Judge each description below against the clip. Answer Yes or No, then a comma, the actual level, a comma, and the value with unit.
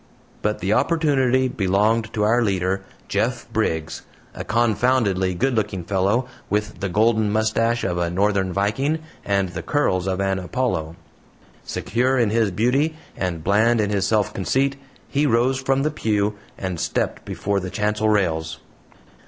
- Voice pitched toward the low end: Yes, low, 105 Hz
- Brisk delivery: No, average, 155 wpm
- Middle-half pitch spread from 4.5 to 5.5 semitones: No, average, 4.0 semitones